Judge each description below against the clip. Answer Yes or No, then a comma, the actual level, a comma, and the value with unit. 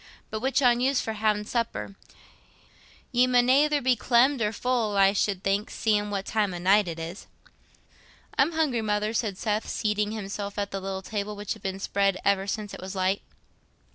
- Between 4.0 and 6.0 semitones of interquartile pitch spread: No, average, 3.2 semitones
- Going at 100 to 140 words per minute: No, average, 190 wpm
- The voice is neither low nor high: No, high, 210 Hz